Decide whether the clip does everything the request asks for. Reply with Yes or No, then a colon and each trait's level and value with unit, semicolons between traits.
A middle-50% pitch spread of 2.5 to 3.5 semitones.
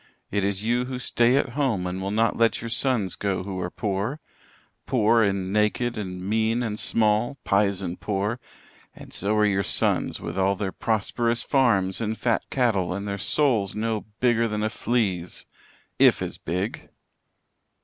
Yes: average, 3.2 semitones